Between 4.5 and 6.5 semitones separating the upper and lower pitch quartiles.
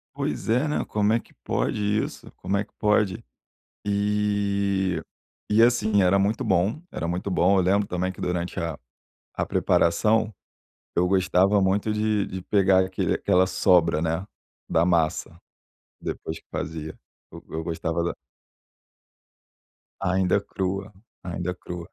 No: narrow, 2.6 semitones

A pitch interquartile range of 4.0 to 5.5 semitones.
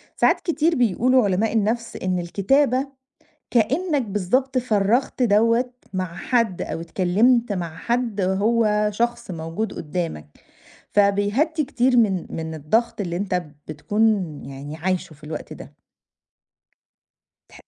Yes: average, 5.0 semitones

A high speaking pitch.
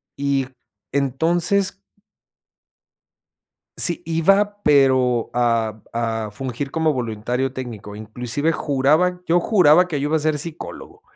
No: medium, 140 Hz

